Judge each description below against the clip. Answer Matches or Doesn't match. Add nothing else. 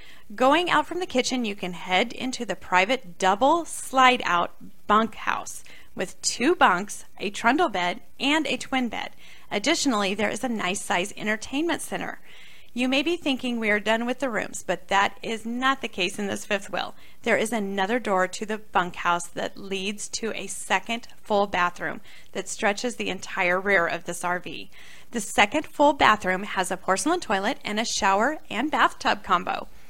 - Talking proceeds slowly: Doesn't match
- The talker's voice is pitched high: Matches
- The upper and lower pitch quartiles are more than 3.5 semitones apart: Matches